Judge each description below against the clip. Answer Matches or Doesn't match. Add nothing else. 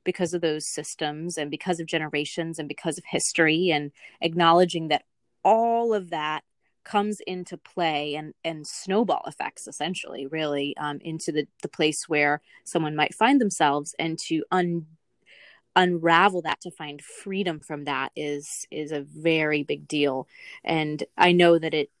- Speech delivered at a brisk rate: Doesn't match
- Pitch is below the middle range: Doesn't match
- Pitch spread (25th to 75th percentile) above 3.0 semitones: Doesn't match